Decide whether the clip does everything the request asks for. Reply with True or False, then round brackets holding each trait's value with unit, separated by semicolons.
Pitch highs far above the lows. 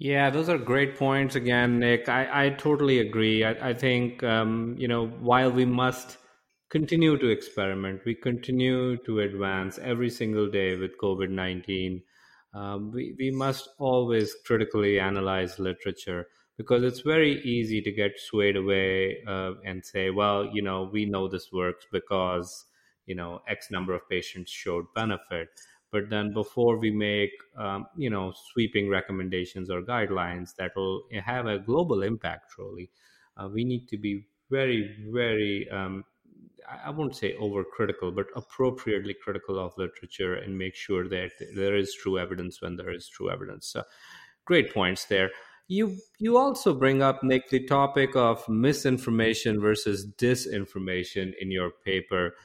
False (4.7 semitones)